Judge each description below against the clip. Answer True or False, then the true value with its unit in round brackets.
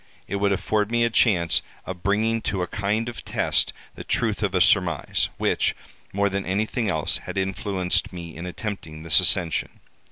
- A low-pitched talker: True (100 Hz)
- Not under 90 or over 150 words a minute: False (180 wpm)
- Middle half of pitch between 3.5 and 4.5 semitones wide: False (3.0 semitones)